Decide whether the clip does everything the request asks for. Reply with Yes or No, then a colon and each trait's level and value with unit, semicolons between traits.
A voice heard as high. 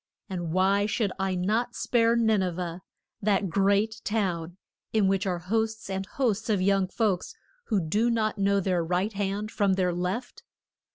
Yes: high, 195 Hz